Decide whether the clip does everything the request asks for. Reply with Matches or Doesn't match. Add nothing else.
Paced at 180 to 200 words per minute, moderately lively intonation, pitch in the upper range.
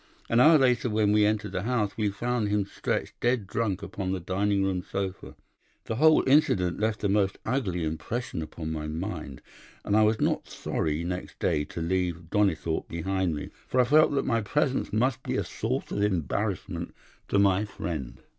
Doesn't match